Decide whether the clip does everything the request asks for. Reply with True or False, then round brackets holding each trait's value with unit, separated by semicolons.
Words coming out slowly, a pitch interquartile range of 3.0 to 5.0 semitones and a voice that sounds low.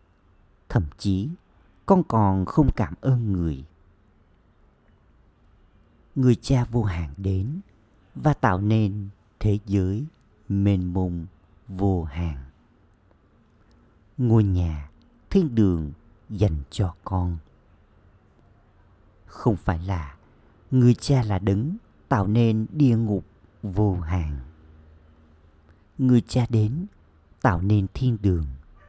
True (100 wpm; 4.7 semitones; 100 Hz)